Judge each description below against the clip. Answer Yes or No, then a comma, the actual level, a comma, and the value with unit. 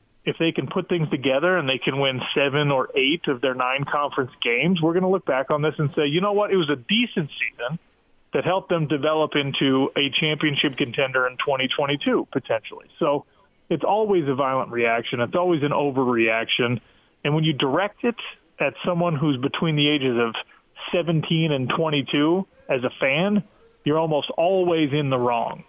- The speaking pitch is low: No, medium, 150 Hz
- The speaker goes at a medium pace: Yes, average, 185 wpm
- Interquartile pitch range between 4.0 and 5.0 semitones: Yes, average, 4.4 semitones